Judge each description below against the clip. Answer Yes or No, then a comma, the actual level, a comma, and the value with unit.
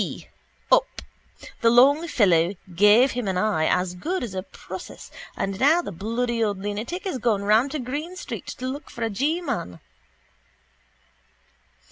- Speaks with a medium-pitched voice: No, high, 230 Hz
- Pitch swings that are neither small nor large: No, wide, 6.0 semitones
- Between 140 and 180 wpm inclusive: Yes, average, 160 wpm